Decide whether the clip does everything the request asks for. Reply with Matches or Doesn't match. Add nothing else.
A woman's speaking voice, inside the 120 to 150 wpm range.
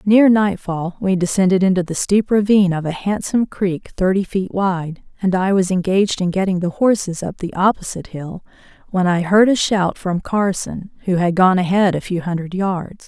Doesn't match